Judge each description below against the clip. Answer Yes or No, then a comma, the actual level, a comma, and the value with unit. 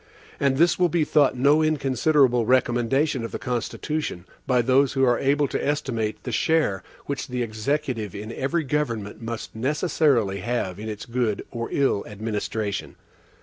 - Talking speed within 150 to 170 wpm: Yes, average, 155 wpm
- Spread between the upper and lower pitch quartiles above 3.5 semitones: Yes, average, 4.4 semitones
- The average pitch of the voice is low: Yes, low, 125 Hz